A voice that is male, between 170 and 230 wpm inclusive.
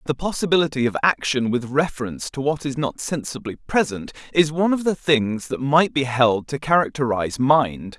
Yes: male; average, 180 wpm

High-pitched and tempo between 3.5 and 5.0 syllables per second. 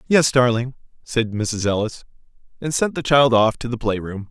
No: low, 120 Hz; 4.8 syllables/s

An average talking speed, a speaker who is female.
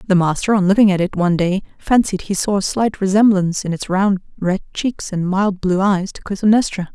No: fast, 215 wpm; female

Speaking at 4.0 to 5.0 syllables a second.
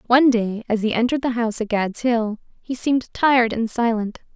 No: 5.8 syllables/s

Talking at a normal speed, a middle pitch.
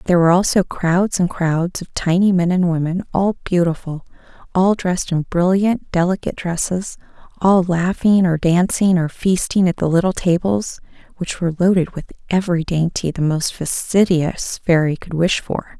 Yes: average, 160 wpm; medium, 175 Hz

